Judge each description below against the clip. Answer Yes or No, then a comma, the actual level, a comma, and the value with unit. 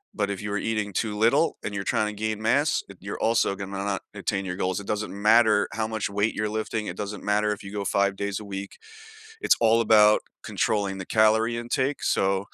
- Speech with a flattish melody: Yes, narrow, 1.7 semitones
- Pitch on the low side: Yes, low, 105 Hz